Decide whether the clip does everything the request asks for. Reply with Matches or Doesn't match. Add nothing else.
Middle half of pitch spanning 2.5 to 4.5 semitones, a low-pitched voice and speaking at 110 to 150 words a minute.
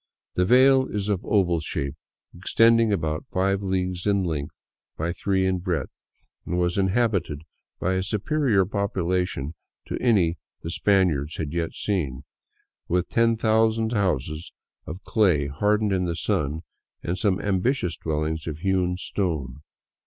Matches